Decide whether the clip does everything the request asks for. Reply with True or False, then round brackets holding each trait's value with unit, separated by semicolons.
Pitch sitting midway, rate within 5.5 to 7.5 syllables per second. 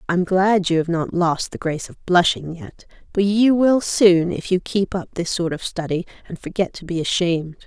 False (180 Hz; 4.9 syllables/s)